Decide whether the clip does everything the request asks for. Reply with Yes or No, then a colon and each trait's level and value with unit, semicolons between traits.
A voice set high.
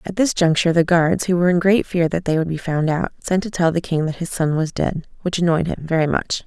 No: medium, 170 Hz